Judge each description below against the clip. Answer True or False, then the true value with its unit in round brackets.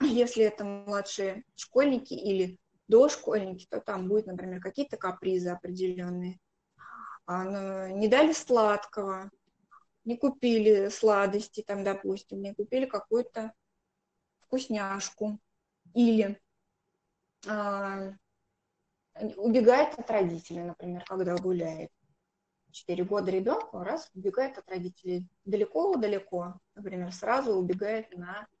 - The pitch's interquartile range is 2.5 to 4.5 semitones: True (2.9 semitones)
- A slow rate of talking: True (95 wpm)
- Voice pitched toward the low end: False (200 Hz)